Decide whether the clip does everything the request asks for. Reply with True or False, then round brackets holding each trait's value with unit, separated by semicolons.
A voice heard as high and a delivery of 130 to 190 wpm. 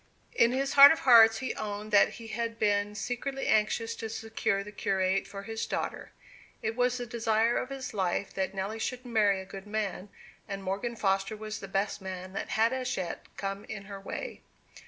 False (215 Hz; 200 wpm)